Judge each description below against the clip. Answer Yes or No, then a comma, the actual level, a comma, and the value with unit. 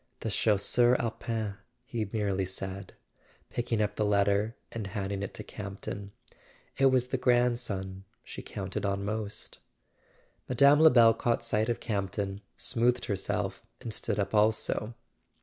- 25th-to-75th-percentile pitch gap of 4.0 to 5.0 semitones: No, average, 3.1 semitones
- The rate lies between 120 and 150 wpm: Yes, average, 140 wpm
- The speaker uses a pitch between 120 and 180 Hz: No, low, 110 Hz